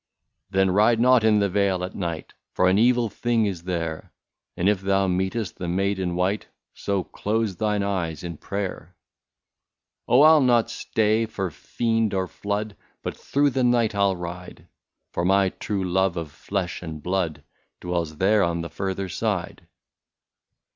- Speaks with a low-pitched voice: Yes, very low, 95 Hz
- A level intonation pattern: No, average, 3.2 semitones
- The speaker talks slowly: No, average, 175 wpm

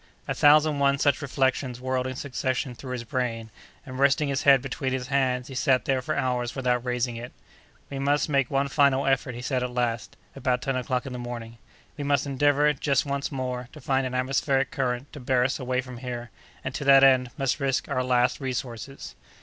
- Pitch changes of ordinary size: No, narrow, 1.7 semitones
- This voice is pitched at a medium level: No, low, 130 Hz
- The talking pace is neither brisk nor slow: No, fast, 210 wpm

